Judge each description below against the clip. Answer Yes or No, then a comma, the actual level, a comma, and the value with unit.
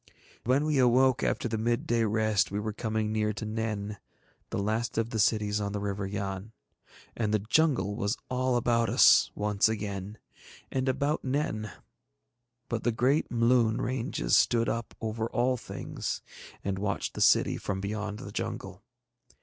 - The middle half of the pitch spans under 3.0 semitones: Yes, narrow, 2.5 semitones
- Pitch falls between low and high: No, low, 110 Hz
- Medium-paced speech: Yes, average, 160 wpm